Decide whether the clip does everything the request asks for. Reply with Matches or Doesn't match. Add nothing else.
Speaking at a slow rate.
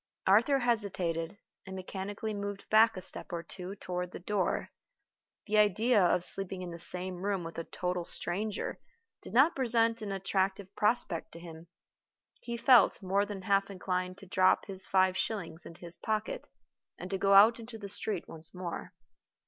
Doesn't match